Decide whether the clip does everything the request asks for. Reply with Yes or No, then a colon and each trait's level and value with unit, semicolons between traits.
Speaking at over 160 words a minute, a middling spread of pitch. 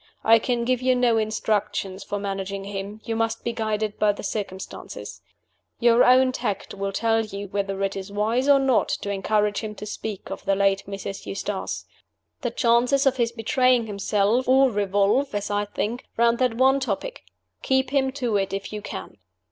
Yes: average, 185 wpm; average, 3.7 semitones